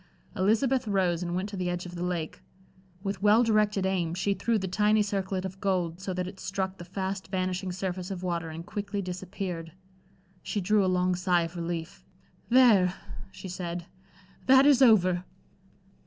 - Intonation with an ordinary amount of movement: No, narrow, 2.2 semitones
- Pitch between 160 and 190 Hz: Yes, medium, 185 Hz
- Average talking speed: Yes, average, 175 wpm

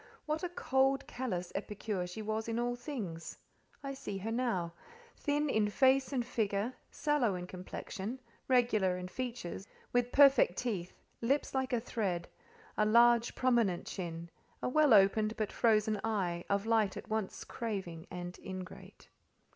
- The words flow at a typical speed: Yes, average, 150 wpm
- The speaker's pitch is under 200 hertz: No, high, 220 Hz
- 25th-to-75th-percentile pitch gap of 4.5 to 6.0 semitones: Yes, average, 4.9 semitones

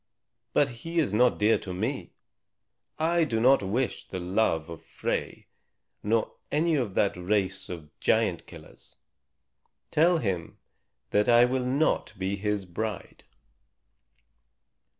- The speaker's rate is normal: No, slow, 130 wpm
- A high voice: No, low, 110 Hz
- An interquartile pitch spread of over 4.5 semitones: Yes, wide, 5.6 semitones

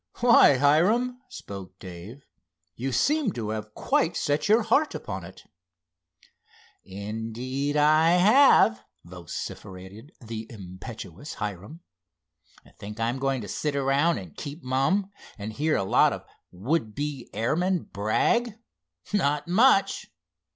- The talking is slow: Yes, slow, 120 wpm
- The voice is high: No, low, 135 Hz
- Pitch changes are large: Yes, wide, 7.7 semitones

